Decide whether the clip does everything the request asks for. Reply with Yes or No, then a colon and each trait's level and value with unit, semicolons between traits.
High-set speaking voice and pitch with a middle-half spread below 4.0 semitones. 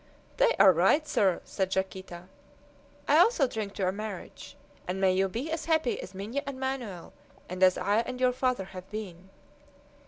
No: high, 200 Hz; wide, 5.5 semitones